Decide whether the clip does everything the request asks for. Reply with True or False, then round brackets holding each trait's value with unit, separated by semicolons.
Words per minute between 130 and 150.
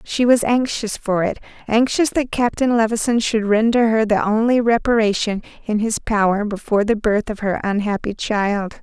False (165 wpm)